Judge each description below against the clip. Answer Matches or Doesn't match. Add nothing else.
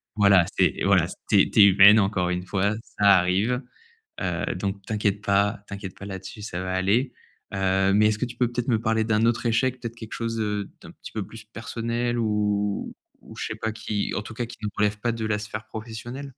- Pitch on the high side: Doesn't match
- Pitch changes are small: Matches